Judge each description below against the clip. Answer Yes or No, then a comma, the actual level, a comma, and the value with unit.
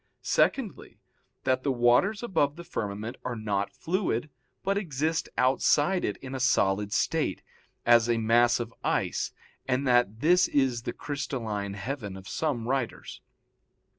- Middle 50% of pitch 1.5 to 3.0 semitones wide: No, average, 4.4 semitones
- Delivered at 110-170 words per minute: Yes, average, 140 wpm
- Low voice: Yes, low, 125 Hz